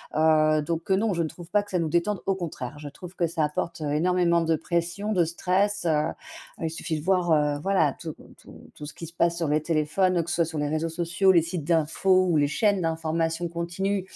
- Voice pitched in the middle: Yes, medium, 170 Hz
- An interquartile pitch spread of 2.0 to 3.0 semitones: Yes, narrow, 2.5 semitones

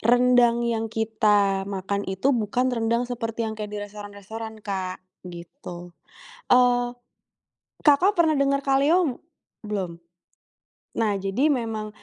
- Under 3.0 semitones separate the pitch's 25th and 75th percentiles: No, average, 3.4 semitones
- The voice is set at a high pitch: Yes, high, 225 Hz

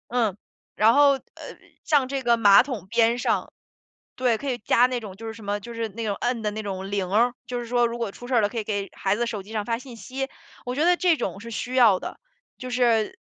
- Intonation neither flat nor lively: Yes, average, 3.1 semitones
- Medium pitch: No, high, 230 Hz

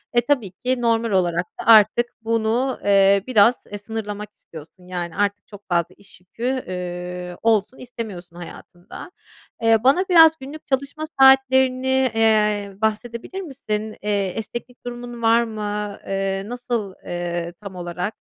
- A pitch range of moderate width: Yes, average, 4.1 semitones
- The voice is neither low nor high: No, high, 215 Hz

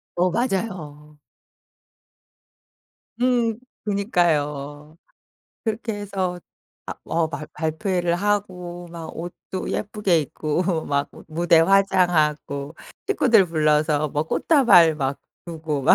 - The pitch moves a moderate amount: Yes, average, 4.4 semitones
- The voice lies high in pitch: No, medium, 170 Hz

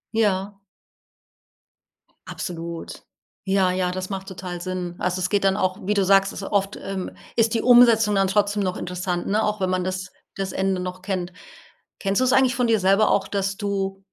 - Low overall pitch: No, high, 195 Hz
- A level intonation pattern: Yes, narrow, 1.9 semitones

